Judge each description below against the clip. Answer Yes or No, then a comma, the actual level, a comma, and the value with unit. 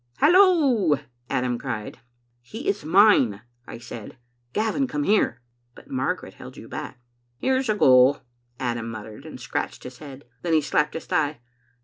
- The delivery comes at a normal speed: Yes, average, 150 wpm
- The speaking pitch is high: No, medium, 145 Hz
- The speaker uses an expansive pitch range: Yes, wide, 8.9 semitones